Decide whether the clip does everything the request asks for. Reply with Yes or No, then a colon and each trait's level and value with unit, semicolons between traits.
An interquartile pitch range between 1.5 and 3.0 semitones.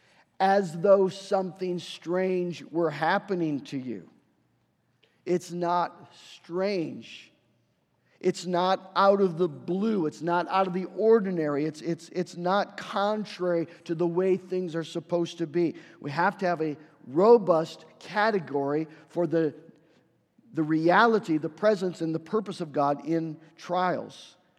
Yes: narrow, 2.6 semitones